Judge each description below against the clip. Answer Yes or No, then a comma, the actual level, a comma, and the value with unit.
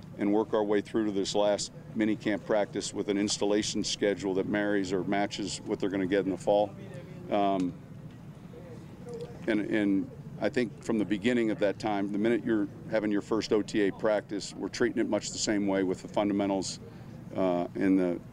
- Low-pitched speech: Yes, low, 105 Hz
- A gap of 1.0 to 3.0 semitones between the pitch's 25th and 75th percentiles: Yes, average, 2.7 semitones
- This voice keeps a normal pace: Yes, average, 195 wpm